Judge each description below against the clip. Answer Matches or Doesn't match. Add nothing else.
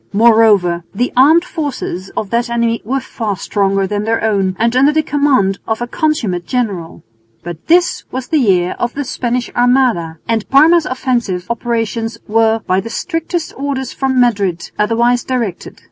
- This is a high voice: Matches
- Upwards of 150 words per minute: Matches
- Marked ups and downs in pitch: Doesn't match